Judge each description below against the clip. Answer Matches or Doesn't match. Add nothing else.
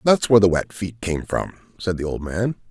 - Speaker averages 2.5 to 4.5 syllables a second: Doesn't match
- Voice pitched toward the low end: Matches